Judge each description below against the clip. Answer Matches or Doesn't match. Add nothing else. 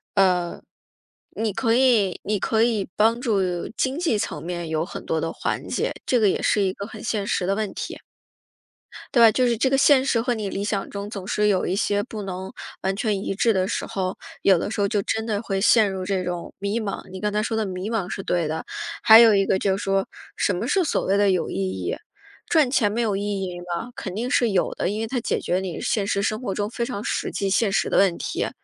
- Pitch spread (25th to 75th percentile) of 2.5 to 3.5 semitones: Matches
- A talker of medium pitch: Doesn't match